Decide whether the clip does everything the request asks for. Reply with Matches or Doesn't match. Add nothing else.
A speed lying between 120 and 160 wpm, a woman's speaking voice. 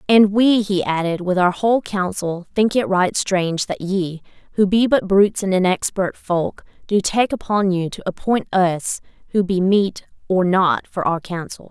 Doesn't match